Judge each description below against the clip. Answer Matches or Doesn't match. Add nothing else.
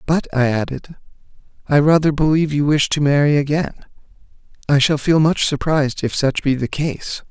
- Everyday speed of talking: Matches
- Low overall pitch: Doesn't match